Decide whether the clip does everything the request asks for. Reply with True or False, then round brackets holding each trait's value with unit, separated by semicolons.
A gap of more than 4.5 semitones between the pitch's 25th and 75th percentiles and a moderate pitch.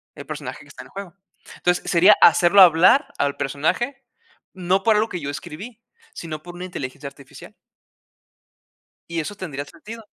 True (5.1 semitones; 175 Hz)